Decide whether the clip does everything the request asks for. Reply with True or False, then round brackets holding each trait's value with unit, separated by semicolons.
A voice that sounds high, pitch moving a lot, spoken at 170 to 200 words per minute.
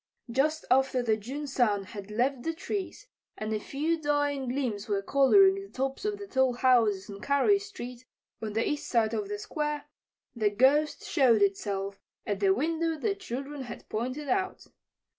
True (260 Hz; 5.7 semitones; 175 wpm)